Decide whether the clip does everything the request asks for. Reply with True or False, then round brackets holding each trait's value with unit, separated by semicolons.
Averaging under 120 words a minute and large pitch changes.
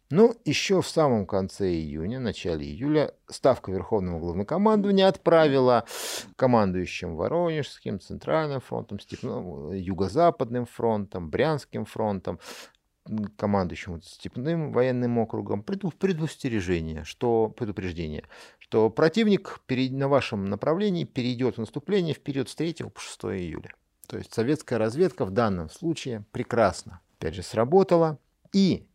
True (110 wpm; 7.8 semitones)